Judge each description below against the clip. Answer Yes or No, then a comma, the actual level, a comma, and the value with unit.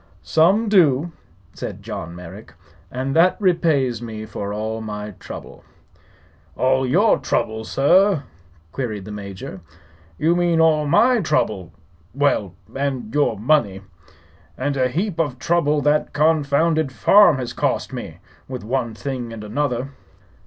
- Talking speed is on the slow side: Yes, slow, 130 wpm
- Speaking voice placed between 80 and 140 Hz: Yes, low, 135 Hz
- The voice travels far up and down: Yes, wide, 6.3 semitones